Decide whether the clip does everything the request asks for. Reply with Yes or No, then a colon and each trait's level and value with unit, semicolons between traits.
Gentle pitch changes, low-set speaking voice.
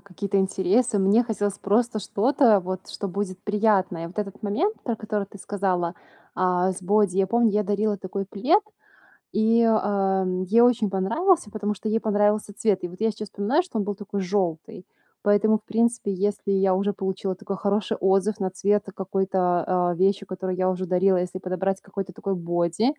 No: narrow, 2.2 semitones; high, 200 Hz